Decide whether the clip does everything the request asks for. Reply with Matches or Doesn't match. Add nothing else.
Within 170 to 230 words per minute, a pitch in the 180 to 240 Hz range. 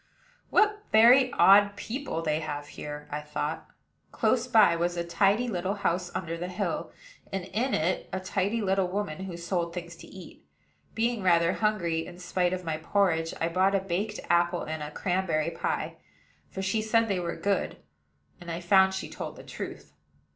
Matches